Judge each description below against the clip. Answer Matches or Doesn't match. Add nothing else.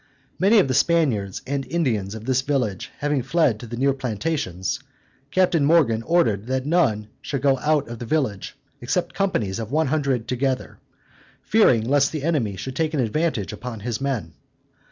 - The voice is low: Matches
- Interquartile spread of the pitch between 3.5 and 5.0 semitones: Doesn't match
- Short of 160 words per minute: Doesn't match